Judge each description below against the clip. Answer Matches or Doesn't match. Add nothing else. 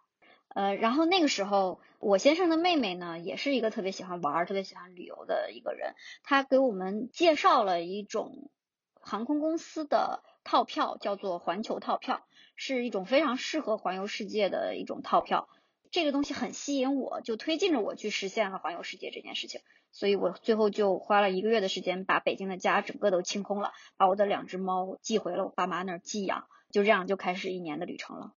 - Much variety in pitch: Matches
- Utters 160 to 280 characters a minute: Doesn't match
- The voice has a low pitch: Doesn't match